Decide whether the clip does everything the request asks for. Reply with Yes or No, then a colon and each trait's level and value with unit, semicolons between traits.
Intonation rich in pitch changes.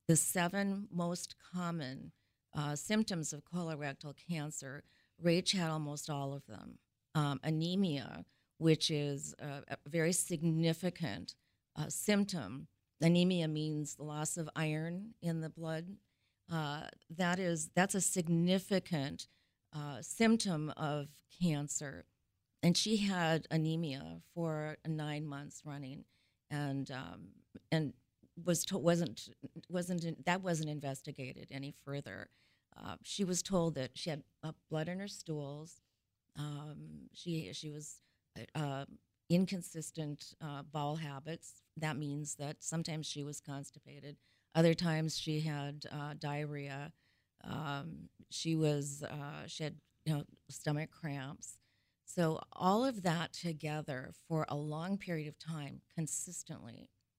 No: average, 3.0 semitones